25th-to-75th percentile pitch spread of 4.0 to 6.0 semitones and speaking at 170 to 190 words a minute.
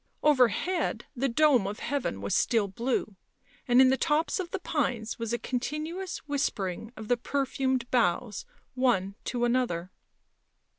No: average, 4.4 semitones; average, 145 wpm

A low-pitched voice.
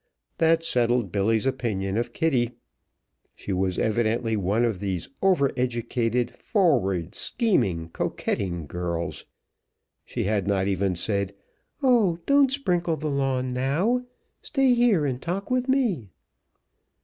Yes: low, 120 Hz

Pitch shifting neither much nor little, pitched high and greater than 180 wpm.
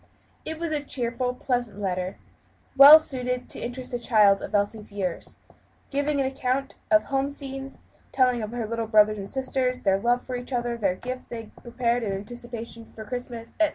Yes: average, 3.5 semitones; high, 245 Hz; average, 190 wpm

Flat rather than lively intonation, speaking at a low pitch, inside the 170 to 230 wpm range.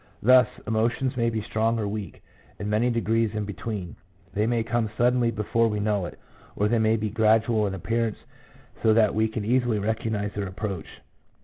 Yes: narrow, 1.8 semitones; low, 110 Hz; average, 185 wpm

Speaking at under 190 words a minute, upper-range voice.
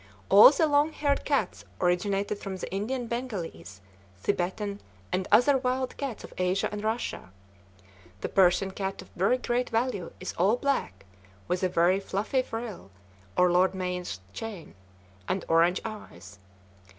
Yes: average, 145 wpm; high, 195 Hz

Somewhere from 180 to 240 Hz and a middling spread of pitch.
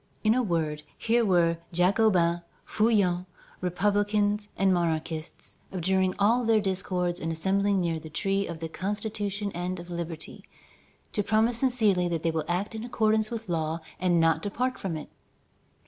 Yes: high, 190 Hz; average, 3.7 semitones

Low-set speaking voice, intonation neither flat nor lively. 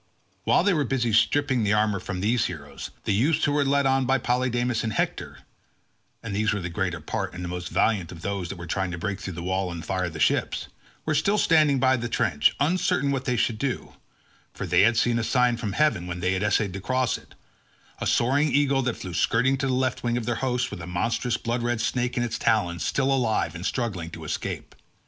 No: low, 115 Hz; wide, 5.7 semitones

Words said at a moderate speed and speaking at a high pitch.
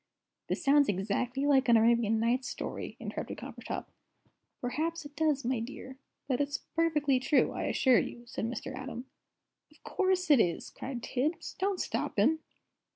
Yes: average, 155 wpm; very high, 265 Hz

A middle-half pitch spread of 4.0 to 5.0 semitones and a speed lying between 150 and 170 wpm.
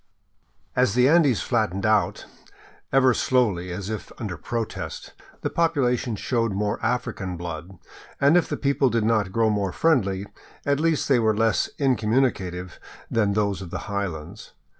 Yes: average, 4.6 semitones; average, 155 wpm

